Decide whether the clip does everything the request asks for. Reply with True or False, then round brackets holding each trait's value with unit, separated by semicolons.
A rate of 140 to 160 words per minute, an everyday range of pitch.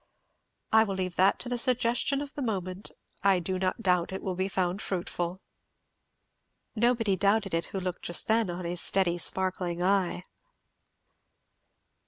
True (155 wpm; 3.4 semitones)